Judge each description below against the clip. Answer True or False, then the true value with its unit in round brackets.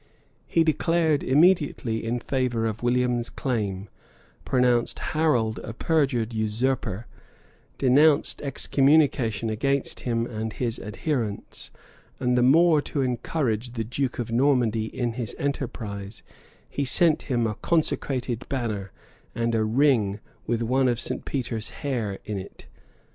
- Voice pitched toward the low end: True (120 Hz)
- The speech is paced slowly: True (125 wpm)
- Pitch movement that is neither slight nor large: True (3.7 semitones)